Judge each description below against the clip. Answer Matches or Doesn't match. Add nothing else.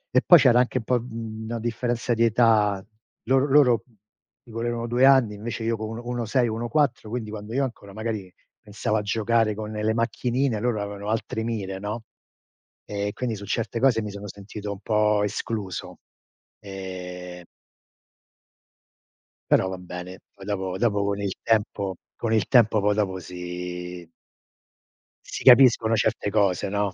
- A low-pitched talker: Matches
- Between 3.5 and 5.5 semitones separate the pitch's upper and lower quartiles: Doesn't match